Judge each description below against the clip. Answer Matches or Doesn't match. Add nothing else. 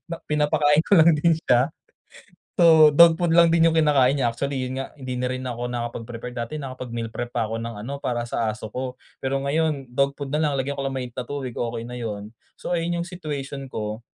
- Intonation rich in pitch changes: Doesn't match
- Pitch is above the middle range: Doesn't match